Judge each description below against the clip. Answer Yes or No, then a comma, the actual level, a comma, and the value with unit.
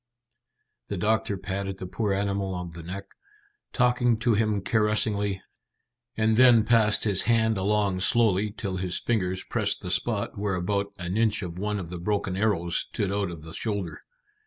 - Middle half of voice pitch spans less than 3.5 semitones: Yes, narrow, 2.6 semitones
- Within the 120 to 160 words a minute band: No, average, 170 wpm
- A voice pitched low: Yes, low, 100 Hz